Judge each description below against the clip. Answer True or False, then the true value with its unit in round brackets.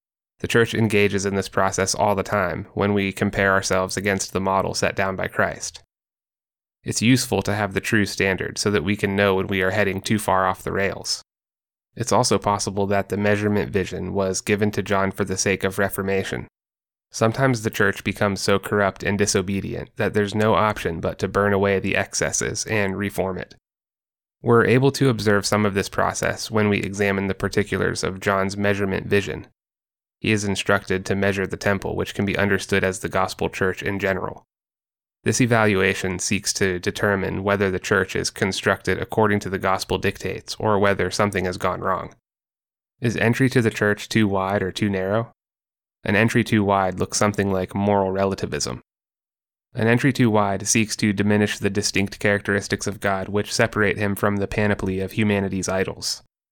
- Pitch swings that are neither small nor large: False (1.5 semitones)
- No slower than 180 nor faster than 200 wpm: True (185 wpm)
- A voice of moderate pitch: False (100 Hz)